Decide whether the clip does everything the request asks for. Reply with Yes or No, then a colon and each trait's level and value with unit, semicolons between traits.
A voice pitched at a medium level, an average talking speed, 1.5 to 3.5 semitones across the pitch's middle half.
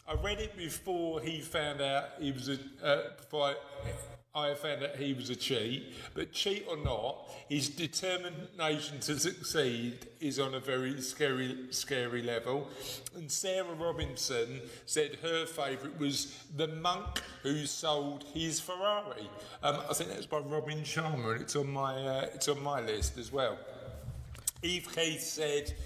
Yes: medium, 145 Hz; average, 160 wpm; average, 3.2 semitones